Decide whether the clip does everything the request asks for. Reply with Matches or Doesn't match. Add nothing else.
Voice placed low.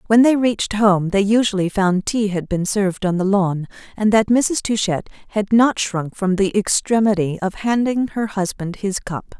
Doesn't match